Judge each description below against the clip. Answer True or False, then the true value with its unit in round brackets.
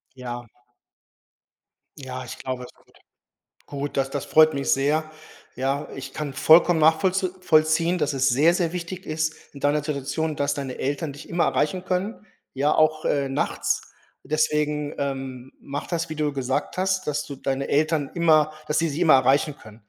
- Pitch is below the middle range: False (150 Hz)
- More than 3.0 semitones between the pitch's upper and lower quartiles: False (2.7 semitones)